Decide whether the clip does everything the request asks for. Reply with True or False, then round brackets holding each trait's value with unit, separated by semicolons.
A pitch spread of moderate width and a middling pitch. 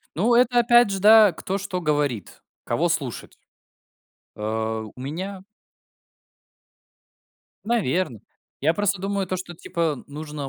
False (5.8 semitones; 180 Hz)